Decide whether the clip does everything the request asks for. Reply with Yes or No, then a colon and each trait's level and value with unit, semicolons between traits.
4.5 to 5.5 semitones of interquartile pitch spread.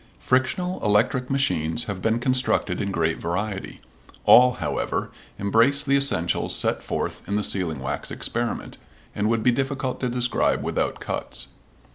Yes: average, 4.8 semitones